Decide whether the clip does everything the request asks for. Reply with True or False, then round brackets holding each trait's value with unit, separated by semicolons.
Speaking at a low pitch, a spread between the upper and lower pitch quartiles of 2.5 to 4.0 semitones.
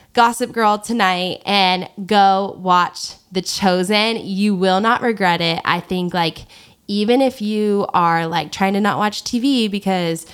False (195 Hz; 2.8 semitones)